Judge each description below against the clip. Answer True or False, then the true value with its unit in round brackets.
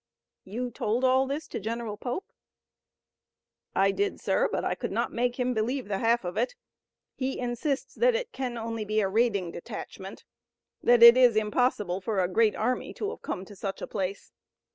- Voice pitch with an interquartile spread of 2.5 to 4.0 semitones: True (3.5 semitones)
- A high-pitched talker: True (235 Hz)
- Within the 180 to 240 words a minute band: True (185 wpm)